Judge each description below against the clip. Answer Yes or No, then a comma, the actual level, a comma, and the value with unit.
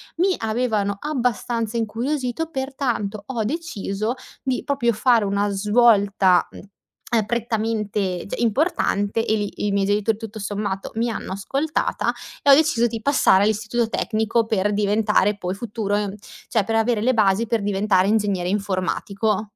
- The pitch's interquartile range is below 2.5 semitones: No, average, 2.9 semitones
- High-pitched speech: Yes, high, 220 Hz